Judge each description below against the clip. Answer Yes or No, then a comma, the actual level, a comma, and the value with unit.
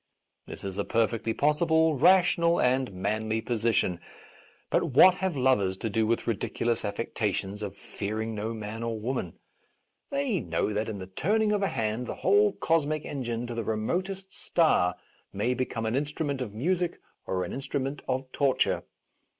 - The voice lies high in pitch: No, low, 120 Hz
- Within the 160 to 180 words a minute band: Yes, average, 165 wpm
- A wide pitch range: Yes, wide, 6.1 semitones